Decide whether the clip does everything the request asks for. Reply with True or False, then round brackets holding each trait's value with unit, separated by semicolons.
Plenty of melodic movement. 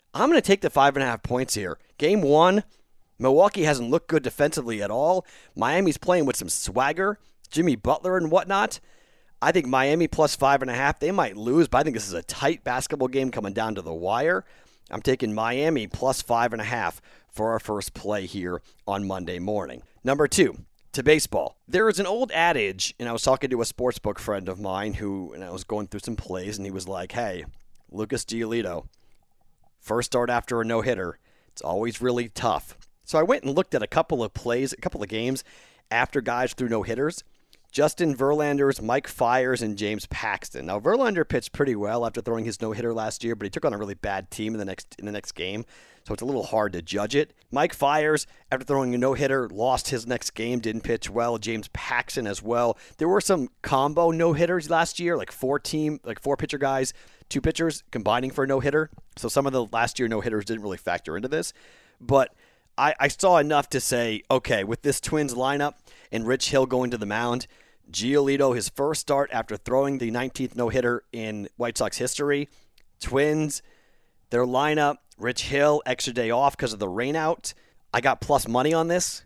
False (4.5 semitones)